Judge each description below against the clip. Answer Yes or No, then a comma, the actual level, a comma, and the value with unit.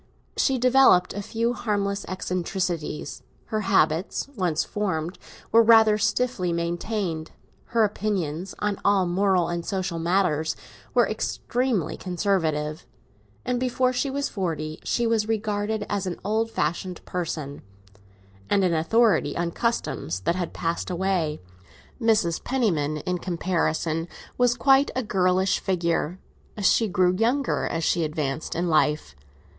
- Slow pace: Yes, slow, 130 wpm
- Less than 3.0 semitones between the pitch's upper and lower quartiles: No, average, 4.6 semitones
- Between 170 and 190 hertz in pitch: Yes, medium, 185 Hz